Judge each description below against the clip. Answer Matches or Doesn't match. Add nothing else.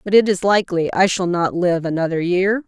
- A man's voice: Doesn't match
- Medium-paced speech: Doesn't match